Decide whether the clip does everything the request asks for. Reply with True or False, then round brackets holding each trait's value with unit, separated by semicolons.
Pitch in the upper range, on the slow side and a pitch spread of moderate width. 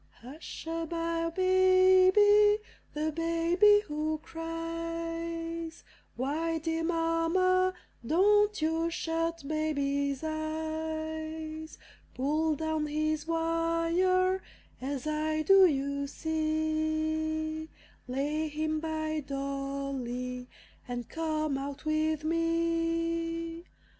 False (320 Hz; 85 wpm; 1.3 semitones)